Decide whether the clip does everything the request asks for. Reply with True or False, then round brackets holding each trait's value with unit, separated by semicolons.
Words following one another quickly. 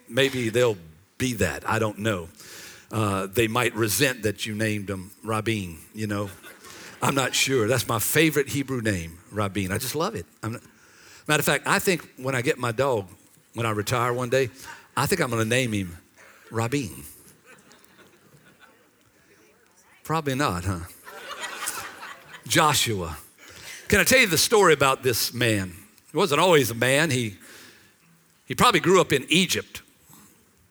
False (160 wpm)